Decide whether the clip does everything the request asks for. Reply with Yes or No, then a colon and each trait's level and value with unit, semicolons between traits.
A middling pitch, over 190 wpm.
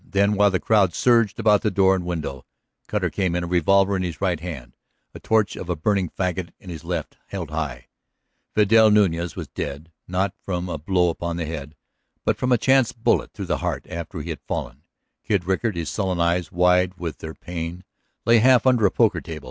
No: very low, 90 Hz; fast, 205 wpm